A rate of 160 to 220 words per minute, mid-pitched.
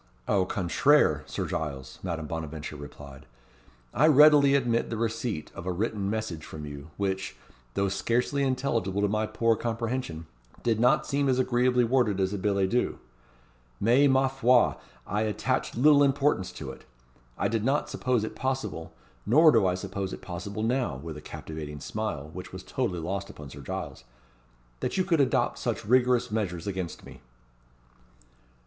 No: average, 165 wpm; low, 105 Hz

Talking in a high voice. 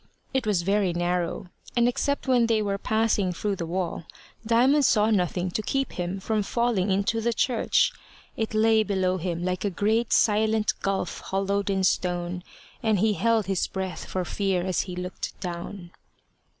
Yes: high, 200 Hz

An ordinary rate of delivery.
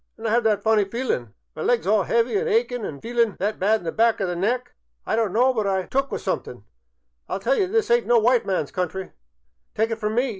No: fast, 260 wpm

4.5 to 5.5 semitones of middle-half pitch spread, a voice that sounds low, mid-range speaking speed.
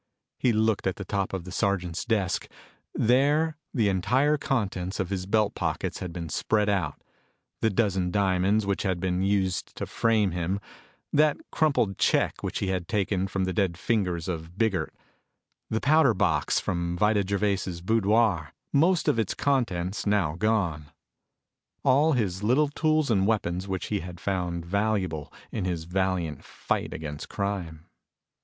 No: average, 3.7 semitones; low, 100 Hz; average, 155 wpm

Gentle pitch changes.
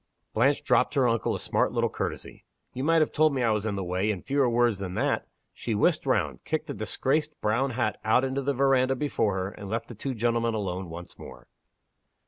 No: average, 4.5 semitones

